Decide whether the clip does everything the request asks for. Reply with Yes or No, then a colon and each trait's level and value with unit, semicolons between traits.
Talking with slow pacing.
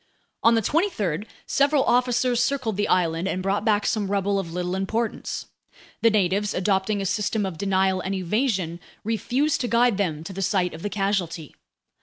No: average, 175 wpm